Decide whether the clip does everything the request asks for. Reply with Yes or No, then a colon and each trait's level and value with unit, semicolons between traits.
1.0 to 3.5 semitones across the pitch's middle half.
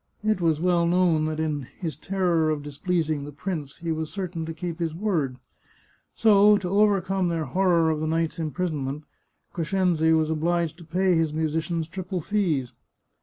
Yes: narrow, 2.6 semitones